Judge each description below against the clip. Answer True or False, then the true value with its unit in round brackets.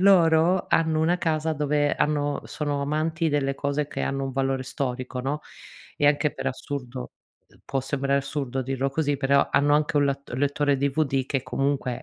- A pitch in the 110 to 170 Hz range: True (140 Hz)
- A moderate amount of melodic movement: False (2.0 semitones)